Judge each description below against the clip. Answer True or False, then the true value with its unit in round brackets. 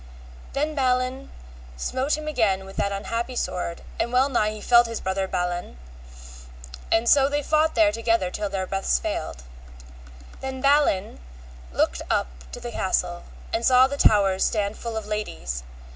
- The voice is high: True (225 Hz)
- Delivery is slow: False (160 wpm)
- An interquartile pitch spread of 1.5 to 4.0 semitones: False (5.4 semitones)